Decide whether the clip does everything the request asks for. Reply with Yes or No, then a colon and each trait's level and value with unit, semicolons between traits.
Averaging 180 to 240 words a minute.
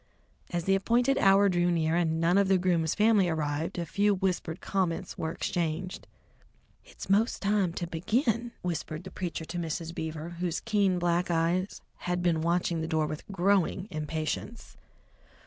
No: average, 165 wpm